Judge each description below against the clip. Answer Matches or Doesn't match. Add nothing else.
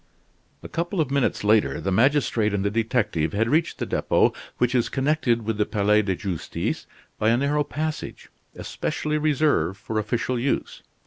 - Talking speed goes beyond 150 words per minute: Matches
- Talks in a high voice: Doesn't match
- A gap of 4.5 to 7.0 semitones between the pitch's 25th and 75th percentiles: Matches